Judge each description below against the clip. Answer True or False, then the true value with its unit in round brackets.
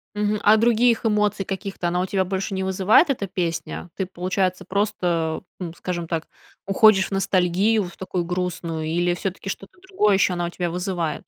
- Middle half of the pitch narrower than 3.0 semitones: True (2.4 semitones)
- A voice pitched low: False (185 Hz)